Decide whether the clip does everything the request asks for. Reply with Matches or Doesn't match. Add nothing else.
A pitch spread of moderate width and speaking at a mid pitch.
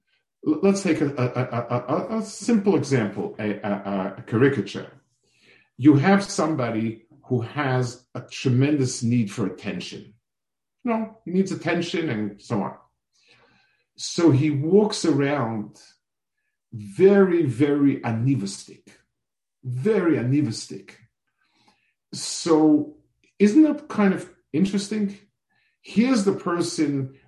Doesn't match